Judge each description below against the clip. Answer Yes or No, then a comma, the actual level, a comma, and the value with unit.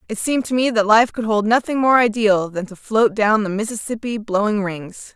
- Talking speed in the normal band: No, fast, 220 wpm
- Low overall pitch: No, high, 215 Hz